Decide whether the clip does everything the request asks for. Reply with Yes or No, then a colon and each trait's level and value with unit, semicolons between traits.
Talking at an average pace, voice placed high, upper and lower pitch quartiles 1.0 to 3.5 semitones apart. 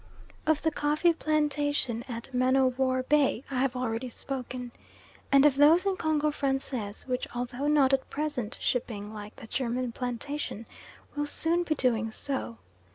Yes: average, 160 wpm; very high, 265 Hz; average, 3.2 semitones